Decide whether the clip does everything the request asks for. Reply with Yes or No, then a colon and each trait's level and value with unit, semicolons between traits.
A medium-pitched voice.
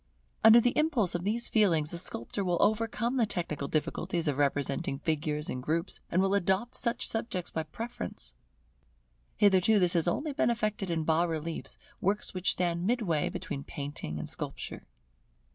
Yes: medium, 175 Hz